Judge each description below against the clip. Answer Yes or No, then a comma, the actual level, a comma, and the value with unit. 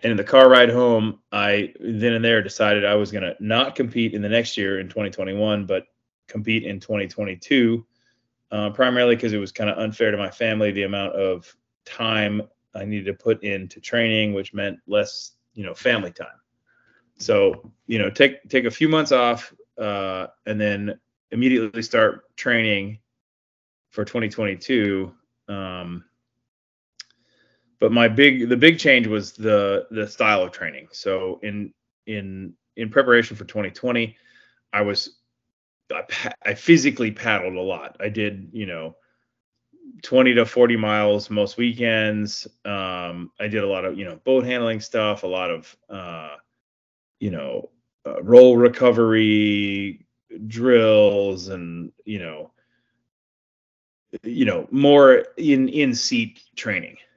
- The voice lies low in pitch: Yes, low, 110 Hz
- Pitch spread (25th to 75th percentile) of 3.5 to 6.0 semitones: No, average, 3.1 semitones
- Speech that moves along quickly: No, average, 150 wpm